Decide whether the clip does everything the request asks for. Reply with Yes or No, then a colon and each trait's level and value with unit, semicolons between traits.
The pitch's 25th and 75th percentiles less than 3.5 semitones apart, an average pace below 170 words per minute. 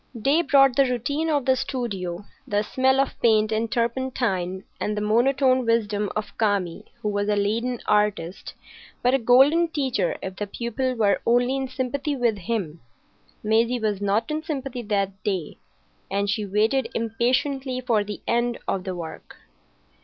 No: average, 4.1 semitones; average, 160 wpm